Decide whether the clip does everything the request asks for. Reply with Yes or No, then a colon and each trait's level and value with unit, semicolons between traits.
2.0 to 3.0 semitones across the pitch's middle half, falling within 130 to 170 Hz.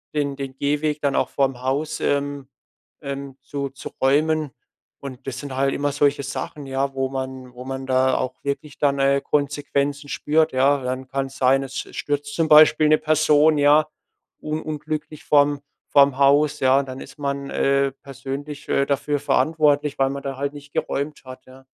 No: narrow, 1.5 semitones; medium, 140 Hz